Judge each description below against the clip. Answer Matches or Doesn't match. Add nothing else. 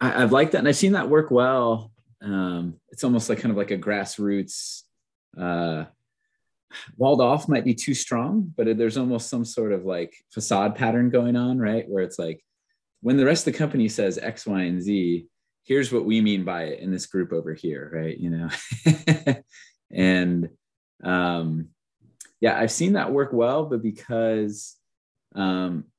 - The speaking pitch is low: Matches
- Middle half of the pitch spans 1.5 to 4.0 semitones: Doesn't match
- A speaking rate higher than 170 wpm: Matches